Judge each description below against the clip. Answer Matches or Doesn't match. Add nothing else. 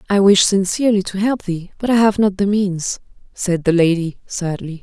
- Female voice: Matches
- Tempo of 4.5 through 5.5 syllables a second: Matches